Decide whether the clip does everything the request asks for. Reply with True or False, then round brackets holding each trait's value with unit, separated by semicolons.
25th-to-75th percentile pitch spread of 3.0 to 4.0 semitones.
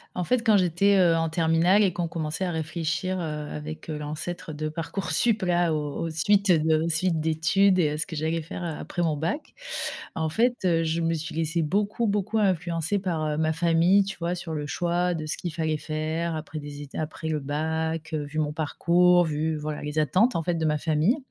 False (2.4 semitones)